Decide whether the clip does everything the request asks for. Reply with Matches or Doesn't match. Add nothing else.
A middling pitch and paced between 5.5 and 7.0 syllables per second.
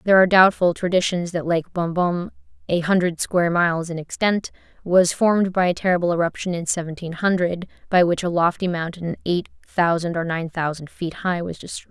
Matches